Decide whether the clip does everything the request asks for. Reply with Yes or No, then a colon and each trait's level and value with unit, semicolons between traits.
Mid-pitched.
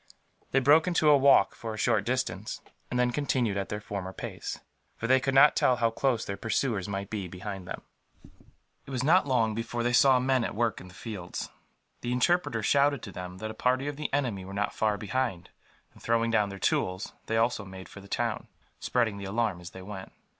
No: low, 115 Hz